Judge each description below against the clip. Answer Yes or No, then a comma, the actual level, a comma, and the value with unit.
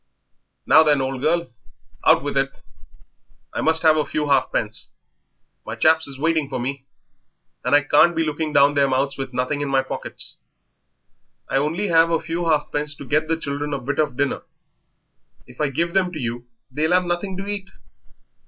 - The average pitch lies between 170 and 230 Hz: No, medium, 150 Hz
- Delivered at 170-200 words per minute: Yes, average, 185 wpm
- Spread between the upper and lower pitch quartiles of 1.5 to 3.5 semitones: Yes, average, 3.0 semitones